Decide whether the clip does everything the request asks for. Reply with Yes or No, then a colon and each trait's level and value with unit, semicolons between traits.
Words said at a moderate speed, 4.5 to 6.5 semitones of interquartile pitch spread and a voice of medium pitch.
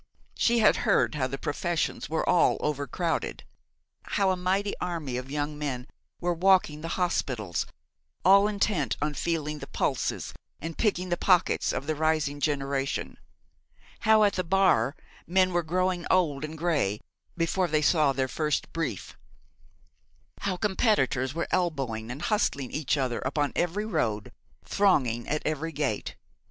Yes: average, 150 wpm; average, 4.8 semitones; medium, 155 Hz